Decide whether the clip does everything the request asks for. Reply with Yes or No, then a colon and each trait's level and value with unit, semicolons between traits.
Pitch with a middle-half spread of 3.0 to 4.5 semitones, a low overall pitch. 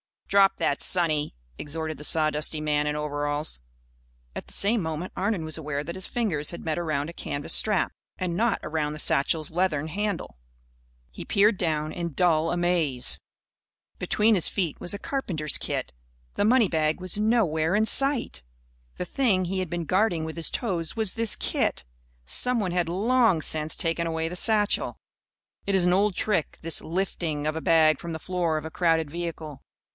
No: average, 3.9 semitones; medium, 170 Hz